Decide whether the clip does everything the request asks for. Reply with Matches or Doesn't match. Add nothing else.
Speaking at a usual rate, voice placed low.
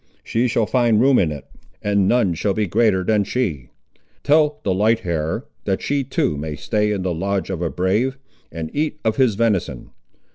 Matches